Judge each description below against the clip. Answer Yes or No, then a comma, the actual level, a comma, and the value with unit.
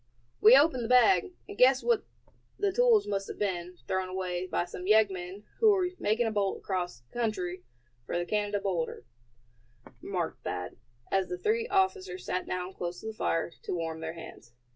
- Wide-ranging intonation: Yes, wide, 6.5 semitones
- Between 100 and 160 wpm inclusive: No, average, 180 wpm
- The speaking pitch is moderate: No, high, 195 Hz